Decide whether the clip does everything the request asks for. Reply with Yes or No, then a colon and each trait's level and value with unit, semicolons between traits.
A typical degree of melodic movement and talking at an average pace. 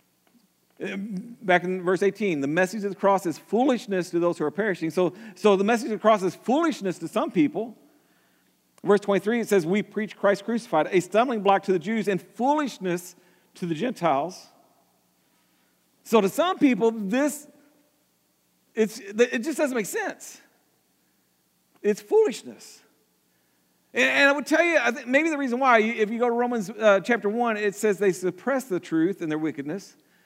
Yes: average, 4.7 semitones; average, 175 wpm